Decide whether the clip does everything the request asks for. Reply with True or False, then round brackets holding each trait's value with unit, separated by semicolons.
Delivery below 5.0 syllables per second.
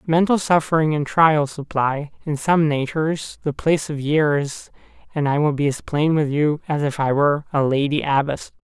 True (4.8 syllables/s)